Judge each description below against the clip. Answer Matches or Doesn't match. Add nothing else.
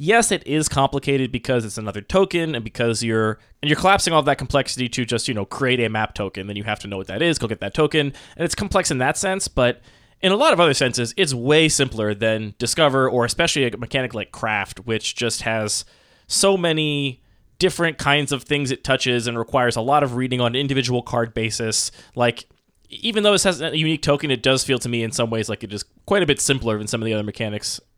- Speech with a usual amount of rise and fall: Matches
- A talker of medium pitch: Doesn't match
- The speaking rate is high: Matches